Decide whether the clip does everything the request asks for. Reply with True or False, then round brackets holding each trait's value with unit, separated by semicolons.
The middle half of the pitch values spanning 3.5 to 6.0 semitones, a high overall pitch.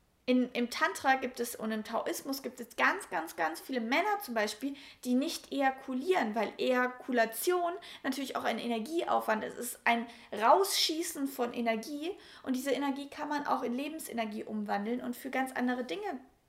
True (3.9 semitones; 260 Hz)